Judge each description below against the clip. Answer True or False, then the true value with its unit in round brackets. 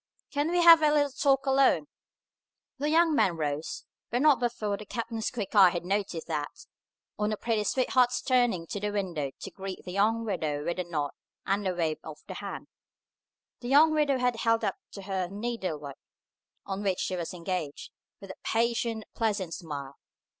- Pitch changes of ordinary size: False (5.7 semitones)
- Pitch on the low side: False (205 Hz)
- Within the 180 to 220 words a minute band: True (190 wpm)